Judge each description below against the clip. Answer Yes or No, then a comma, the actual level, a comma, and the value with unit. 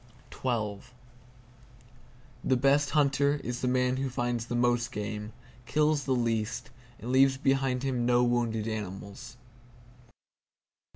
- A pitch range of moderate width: No, narrow, 2.3 semitones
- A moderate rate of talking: No, slow, 115 wpm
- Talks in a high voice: No, low, 125 Hz